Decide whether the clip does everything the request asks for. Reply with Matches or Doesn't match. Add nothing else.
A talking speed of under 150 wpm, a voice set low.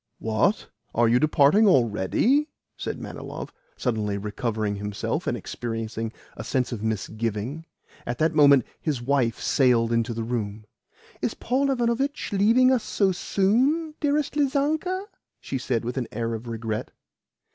Matches